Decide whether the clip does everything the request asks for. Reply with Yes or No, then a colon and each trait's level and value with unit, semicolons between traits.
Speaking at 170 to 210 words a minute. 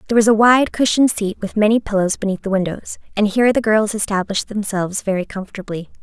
Yes: average, 200 wpm